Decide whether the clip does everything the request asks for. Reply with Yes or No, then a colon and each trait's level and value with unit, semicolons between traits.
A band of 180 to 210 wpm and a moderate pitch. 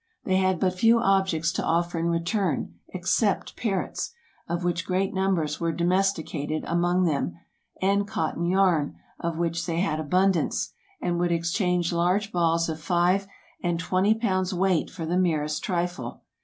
No: average, 155 wpm; medium, 175 Hz